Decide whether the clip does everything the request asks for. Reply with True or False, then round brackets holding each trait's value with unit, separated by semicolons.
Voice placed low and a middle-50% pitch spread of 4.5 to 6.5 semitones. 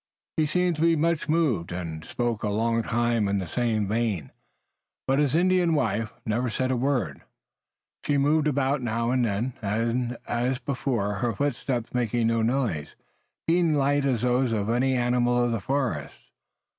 False (120 Hz; 3.7 semitones)